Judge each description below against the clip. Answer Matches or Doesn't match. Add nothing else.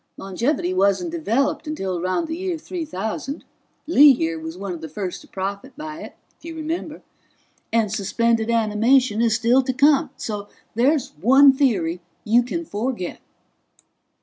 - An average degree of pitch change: Doesn't match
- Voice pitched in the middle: Doesn't match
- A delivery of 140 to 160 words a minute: Matches